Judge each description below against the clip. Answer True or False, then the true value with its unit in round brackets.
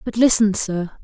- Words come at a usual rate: True (175 wpm)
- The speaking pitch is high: True (205 Hz)